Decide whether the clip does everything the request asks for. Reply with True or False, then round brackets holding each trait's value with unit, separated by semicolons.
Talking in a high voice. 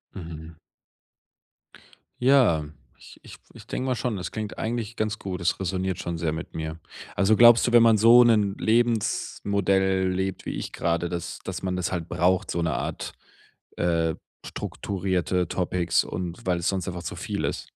False (95 Hz)